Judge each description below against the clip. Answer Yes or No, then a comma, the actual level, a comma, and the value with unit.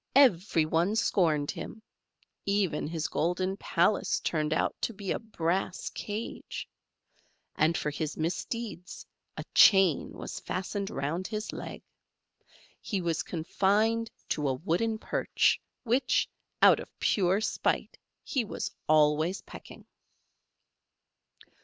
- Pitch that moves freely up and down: No, average, 4.8 semitones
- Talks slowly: Yes, slow, 115 wpm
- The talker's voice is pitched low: No, medium, 185 Hz